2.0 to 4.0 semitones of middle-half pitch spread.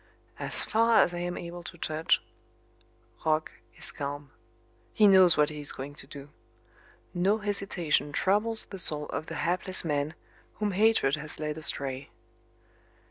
No: average, 4.6 semitones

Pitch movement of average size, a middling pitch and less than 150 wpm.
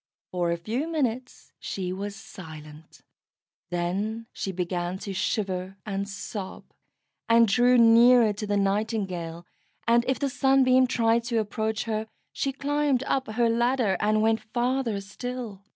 No: average, 4.1 semitones; high, 220 Hz; average, 140 wpm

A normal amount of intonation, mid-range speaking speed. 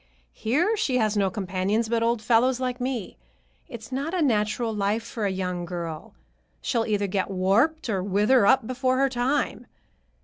Yes: average, 4.4 semitones; average, 170 wpm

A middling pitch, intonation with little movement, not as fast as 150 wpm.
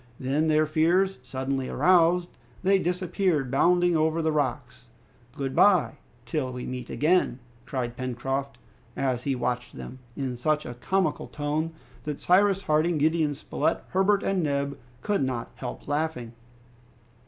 No: medium, 150 Hz; average, 4.9 semitones; average, 140 wpm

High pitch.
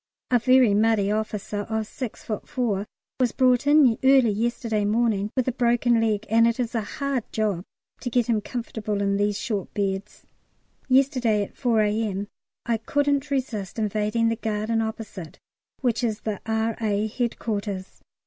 Yes: high, 225 Hz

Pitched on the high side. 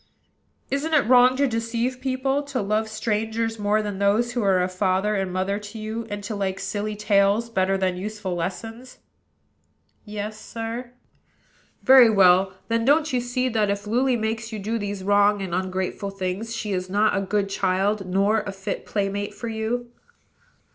Yes: high, 210 Hz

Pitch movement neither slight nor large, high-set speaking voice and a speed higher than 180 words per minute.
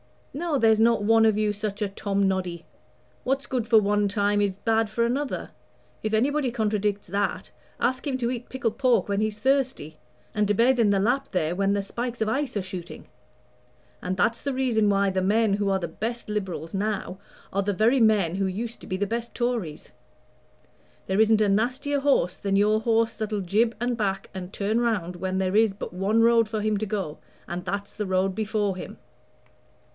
Yes: average, 3.0 semitones; high, 210 Hz; average, 200 wpm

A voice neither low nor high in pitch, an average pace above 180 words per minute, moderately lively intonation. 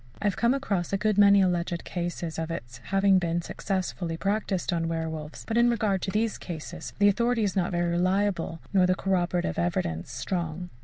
Yes: medium, 180 Hz; average, 190 wpm; average, 3.2 semitones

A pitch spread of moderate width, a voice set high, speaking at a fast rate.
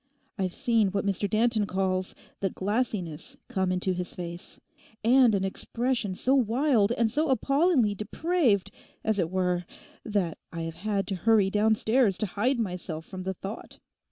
No: average, 3.9 semitones; high, 205 Hz; average, 155 wpm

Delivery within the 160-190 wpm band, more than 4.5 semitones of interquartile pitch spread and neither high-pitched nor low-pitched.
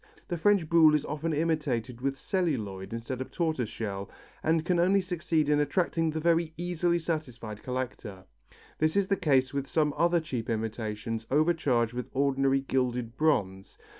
Yes: average, 165 wpm; wide, 5.5 semitones; medium, 145 Hz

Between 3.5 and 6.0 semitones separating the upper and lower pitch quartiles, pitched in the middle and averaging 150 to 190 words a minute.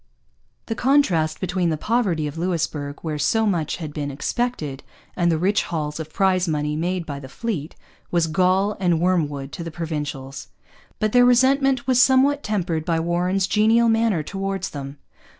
Yes: wide, 5.6 semitones; medium, 175 Hz; average, 170 wpm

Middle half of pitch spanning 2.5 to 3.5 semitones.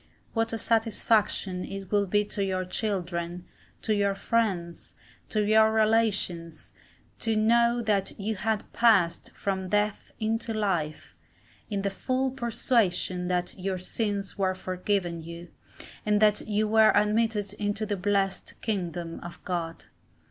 Yes: average, 3.1 semitones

